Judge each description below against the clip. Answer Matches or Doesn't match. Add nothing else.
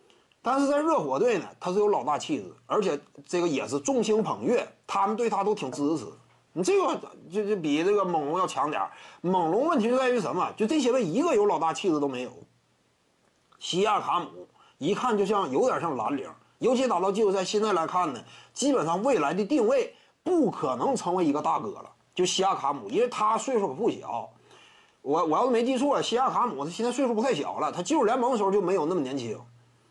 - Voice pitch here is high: Matches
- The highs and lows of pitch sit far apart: Matches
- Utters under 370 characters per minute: Matches